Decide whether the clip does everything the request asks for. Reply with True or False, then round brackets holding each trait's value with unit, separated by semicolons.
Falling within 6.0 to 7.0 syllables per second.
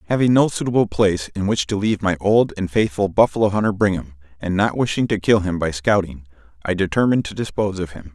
True (6.4 syllables/s)